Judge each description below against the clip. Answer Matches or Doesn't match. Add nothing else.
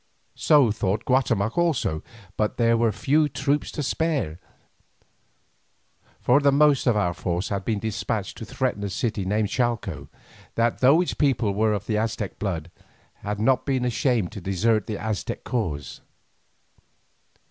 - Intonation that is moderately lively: Matches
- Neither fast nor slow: Matches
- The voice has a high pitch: Doesn't match